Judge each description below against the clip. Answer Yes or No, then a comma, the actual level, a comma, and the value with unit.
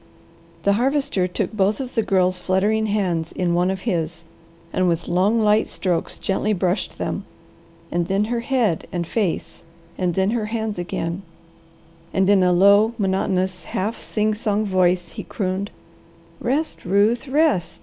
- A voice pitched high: Yes, high, 195 Hz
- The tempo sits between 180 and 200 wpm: No, average, 155 wpm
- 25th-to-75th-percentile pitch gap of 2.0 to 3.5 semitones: Yes, average, 3.1 semitones